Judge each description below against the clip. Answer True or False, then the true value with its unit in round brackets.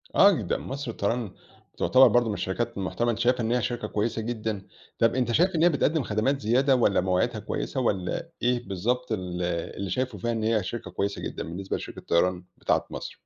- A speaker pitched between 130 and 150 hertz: False (115 Hz)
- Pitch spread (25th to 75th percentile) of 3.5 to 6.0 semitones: True (4.1 semitones)